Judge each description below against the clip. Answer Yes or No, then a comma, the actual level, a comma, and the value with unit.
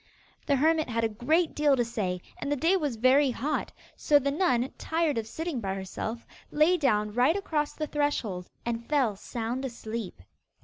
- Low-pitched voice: No, very high, 260 Hz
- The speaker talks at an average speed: Yes, average, 180 wpm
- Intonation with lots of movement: No, average, 5.0 semitones